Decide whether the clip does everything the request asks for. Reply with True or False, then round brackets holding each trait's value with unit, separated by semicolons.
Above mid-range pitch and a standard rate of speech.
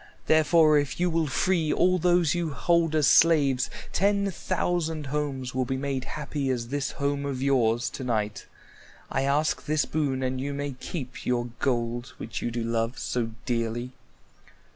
False (140 Hz; 165 wpm)